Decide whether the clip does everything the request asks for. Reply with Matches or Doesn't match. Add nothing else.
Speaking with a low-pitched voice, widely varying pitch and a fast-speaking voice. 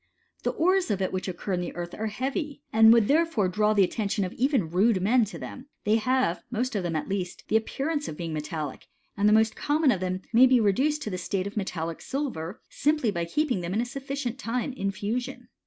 Doesn't match